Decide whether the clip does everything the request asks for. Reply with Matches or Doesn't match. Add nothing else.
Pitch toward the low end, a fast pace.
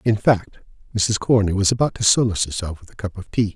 Matches